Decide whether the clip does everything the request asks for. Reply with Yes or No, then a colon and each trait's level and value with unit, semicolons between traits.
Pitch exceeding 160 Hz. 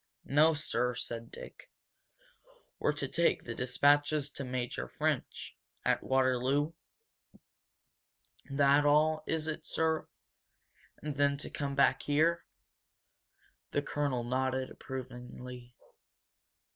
No: medium, 140 Hz